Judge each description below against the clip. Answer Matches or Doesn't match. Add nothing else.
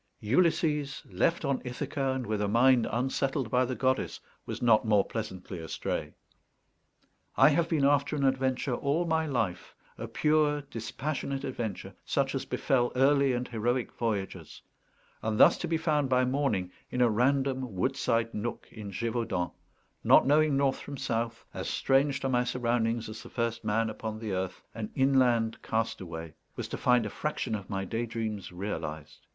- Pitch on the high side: Doesn't match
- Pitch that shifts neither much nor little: Matches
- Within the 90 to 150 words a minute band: Doesn't match